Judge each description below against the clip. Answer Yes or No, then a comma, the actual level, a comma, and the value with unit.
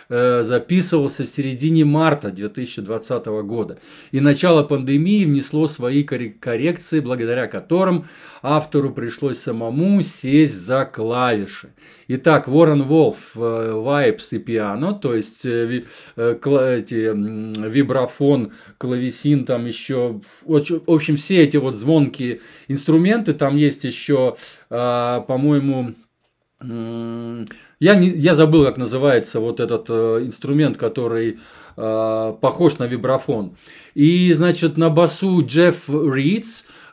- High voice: No, medium, 140 Hz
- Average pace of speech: No, slow, 105 wpm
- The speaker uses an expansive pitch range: No, average, 4.8 semitones